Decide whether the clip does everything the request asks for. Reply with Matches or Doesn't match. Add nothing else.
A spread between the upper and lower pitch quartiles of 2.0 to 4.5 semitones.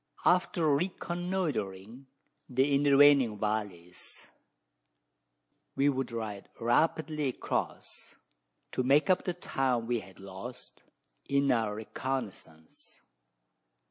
Doesn't match